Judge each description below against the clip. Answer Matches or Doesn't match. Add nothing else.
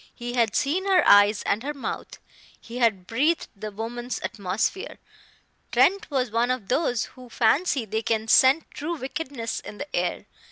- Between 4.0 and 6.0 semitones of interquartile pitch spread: Matches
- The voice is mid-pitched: Doesn't match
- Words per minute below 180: Matches